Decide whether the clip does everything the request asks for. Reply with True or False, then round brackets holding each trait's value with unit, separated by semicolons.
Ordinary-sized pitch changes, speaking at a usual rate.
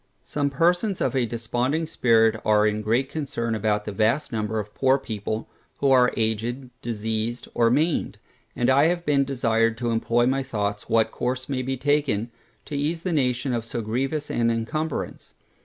True (3.7 semitones; 175 wpm)